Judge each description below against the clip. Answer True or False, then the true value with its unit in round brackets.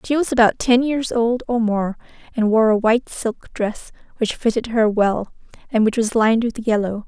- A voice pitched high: True (230 Hz)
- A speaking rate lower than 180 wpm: False (205 wpm)